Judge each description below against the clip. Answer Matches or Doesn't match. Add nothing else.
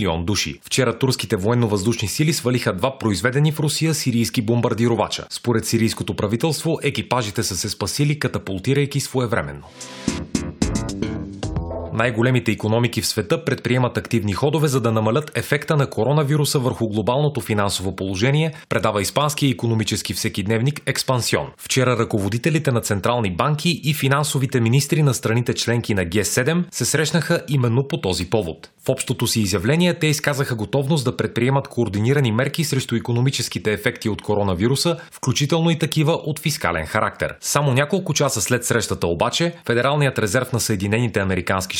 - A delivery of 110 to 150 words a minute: Matches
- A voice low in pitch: Matches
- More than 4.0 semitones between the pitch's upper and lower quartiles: Matches